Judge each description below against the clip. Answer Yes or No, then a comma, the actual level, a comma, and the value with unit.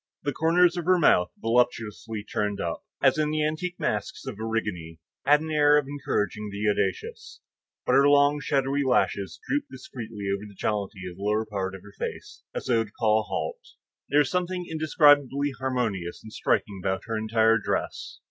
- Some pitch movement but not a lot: No, wide, 6.2 semitones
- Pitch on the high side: No, low, 120 Hz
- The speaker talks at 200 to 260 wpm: No, average, 185 wpm